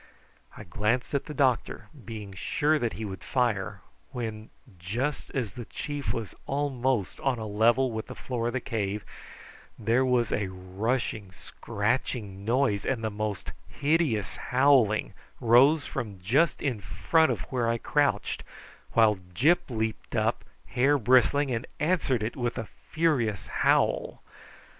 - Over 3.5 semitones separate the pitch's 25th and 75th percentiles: Yes, average, 4.0 semitones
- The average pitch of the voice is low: Yes, low, 120 Hz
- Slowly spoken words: No, average, 150 wpm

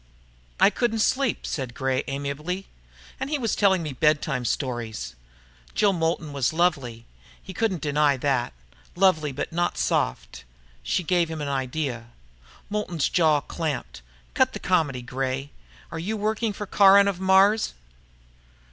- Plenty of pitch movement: Yes, wide, 6.3 semitones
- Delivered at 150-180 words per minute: No, average, 140 wpm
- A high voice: No, medium, 155 Hz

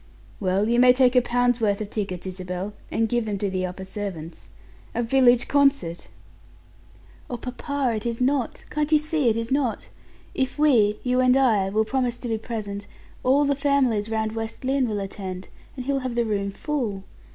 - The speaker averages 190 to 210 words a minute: Yes, average, 195 wpm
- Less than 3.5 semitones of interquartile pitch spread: No, average, 4.2 semitones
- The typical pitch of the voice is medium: No, high, 235 Hz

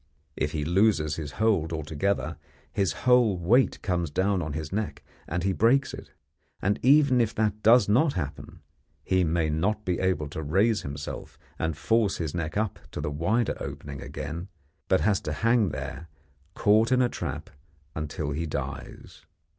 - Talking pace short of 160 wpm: No, average, 165 wpm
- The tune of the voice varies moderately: No, wide, 5.9 semitones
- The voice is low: Yes, very low, 90 Hz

